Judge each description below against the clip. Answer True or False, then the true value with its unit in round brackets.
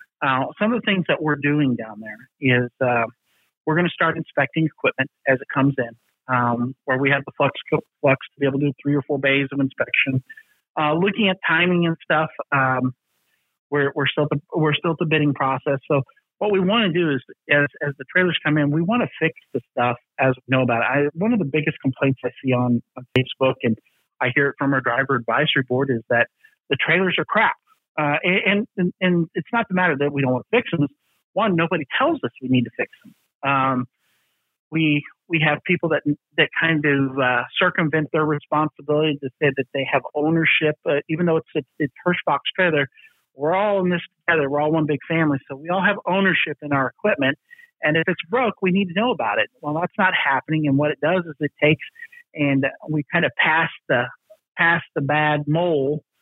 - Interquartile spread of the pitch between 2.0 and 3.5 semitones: False (4.2 semitones)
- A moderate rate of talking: False (220 wpm)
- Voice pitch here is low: False (150 Hz)